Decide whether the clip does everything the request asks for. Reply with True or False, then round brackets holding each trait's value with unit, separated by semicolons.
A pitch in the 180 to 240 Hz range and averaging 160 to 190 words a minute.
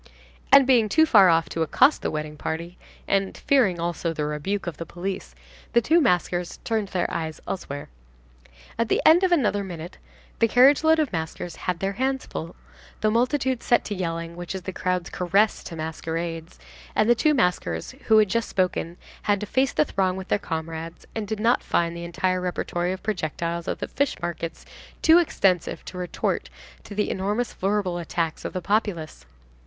True (185 Hz; 185 wpm)